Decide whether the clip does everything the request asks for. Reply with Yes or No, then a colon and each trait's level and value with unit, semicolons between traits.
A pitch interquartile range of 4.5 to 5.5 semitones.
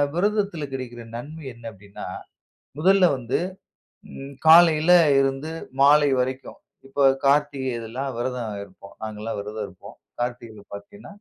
Yes: average, 5.0 semitones